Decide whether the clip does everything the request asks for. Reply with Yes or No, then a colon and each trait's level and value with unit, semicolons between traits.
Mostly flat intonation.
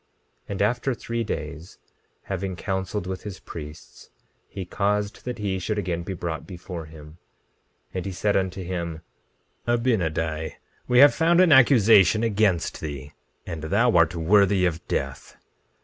No: average, 4.1 semitones